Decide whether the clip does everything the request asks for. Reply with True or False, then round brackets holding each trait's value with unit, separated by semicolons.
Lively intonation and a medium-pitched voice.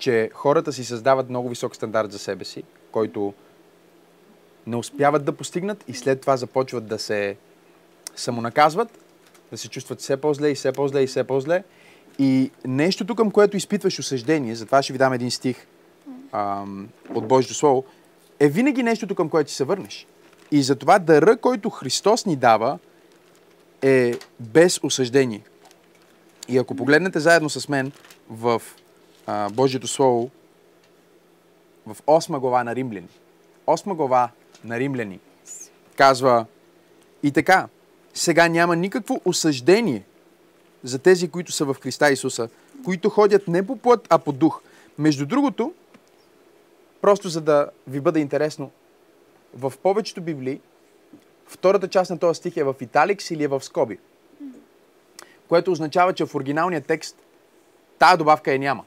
True (6.5 semitones; 150 Hz)